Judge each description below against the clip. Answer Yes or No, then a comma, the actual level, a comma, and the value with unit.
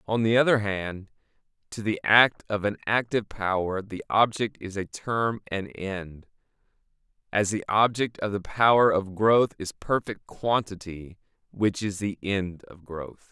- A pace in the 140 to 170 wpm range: Yes, average, 160 wpm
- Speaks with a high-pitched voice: No, low, 100 Hz